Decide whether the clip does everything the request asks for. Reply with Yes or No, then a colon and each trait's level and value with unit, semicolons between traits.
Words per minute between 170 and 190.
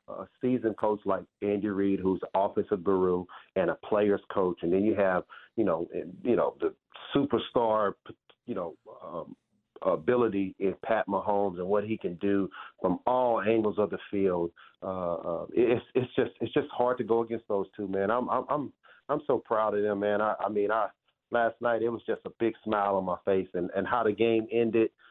No: fast, 205 wpm